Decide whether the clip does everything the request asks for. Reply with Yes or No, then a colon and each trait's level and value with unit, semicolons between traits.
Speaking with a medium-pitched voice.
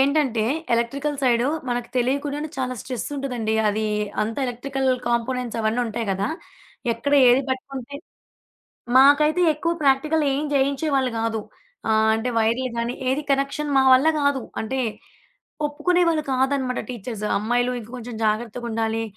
No: very high, 255 Hz